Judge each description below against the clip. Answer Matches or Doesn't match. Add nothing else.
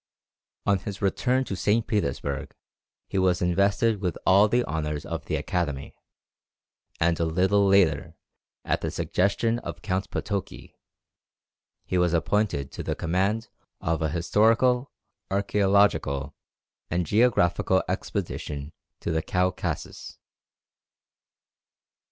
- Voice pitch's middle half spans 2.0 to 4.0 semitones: Matches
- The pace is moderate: Doesn't match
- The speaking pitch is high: Doesn't match